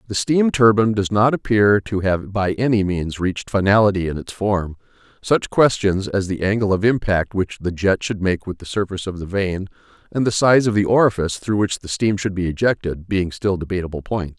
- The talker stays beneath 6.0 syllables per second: Yes, 5.4 syllables/s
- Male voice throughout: Yes, male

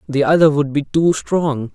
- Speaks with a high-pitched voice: No, medium, 150 Hz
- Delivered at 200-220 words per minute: Yes, fast, 205 wpm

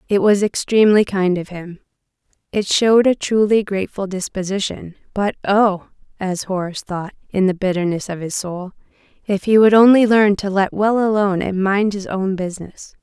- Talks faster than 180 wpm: No, average, 165 wpm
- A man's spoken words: No, female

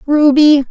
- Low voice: No, very high, 290 Hz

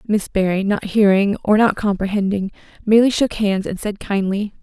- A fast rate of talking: No, average, 170 wpm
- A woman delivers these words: Yes, female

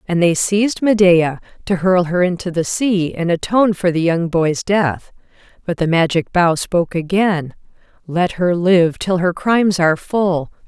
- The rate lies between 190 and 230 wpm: No, average, 175 wpm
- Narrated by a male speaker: No, female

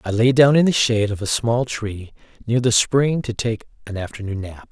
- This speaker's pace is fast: Yes, fast, 230 wpm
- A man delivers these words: Yes, male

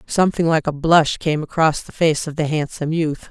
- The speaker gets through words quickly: Yes, fast, 220 wpm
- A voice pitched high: No, medium, 155 Hz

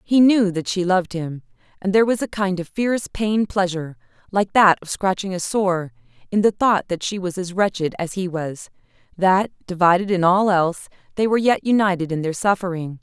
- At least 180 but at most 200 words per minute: Yes, average, 195 wpm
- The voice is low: No, medium, 185 Hz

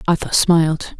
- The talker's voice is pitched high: No, medium, 160 Hz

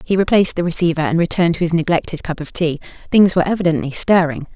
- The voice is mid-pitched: Yes, medium, 170 Hz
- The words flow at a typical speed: No, fast, 210 wpm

